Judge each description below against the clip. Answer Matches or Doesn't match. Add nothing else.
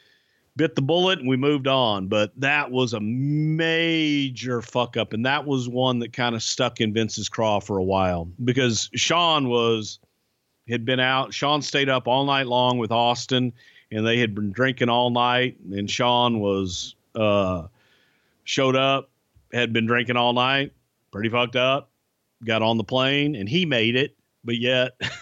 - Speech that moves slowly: Doesn't match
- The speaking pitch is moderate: Doesn't match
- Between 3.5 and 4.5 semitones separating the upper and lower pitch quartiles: Doesn't match